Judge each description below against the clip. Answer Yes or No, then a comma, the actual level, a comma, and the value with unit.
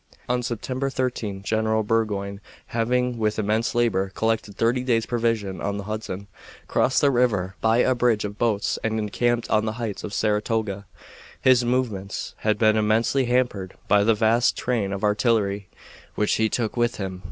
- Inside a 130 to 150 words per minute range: No, average, 165 wpm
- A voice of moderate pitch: No, low, 110 Hz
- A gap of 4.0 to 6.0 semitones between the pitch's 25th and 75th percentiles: No, average, 2.7 semitones